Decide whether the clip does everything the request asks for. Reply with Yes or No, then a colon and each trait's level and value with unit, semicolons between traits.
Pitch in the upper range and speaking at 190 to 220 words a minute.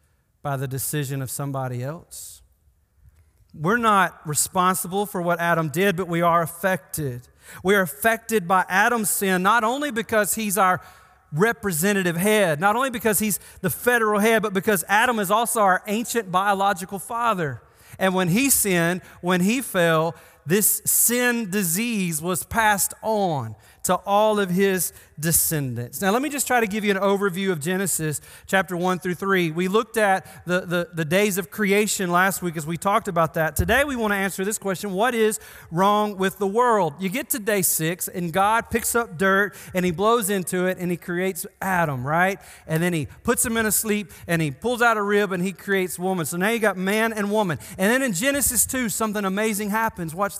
Yes: high, 195 Hz; average, 195 wpm